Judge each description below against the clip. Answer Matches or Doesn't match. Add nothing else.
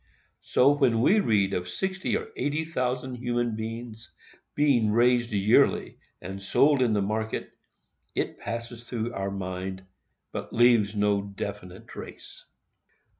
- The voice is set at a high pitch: Doesn't match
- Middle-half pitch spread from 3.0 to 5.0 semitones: Matches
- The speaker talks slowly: Matches